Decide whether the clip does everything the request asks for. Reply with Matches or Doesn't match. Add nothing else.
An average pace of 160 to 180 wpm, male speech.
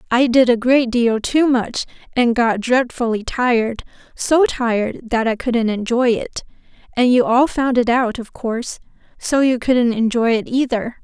Doesn't match